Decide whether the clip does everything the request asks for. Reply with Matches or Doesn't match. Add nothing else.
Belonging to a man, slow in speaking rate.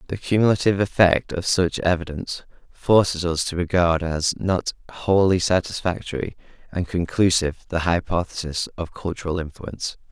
Matches